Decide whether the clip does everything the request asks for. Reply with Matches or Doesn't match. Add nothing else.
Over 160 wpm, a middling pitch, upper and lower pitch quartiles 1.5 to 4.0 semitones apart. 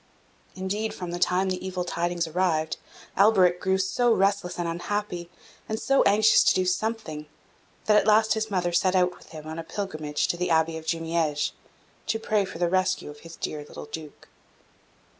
Matches